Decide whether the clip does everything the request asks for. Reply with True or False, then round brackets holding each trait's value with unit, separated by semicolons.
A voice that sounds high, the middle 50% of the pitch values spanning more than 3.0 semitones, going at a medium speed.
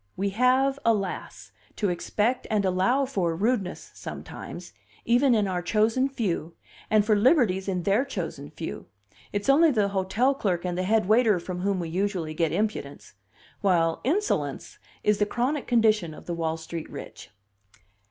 True (205 Hz; 5.0 semitones; 160 wpm)